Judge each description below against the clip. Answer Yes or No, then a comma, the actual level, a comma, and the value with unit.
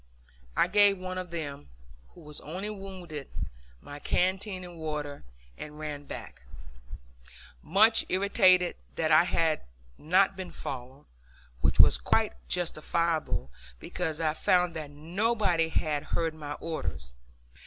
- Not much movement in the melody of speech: No, average, 3.4 semitones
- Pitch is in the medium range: Yes, medium, 165 Hz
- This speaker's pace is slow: Yes, slow, 125 wpm